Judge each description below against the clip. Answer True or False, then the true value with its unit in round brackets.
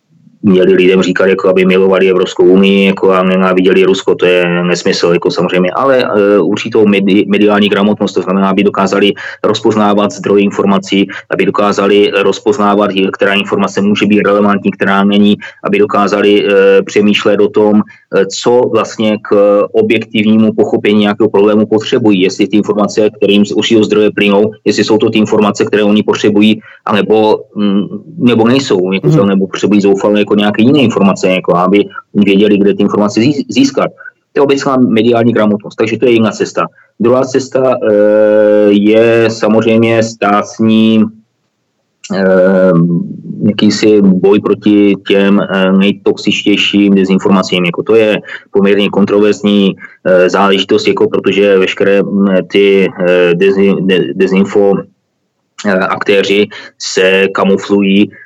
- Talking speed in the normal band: True (130 wpm)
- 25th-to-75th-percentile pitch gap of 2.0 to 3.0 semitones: False (1.4 semitones)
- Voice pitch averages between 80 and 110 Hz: True (100 Hz)